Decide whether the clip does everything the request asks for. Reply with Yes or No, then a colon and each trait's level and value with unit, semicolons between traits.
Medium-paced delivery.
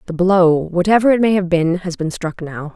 Yes: average, 195 wpm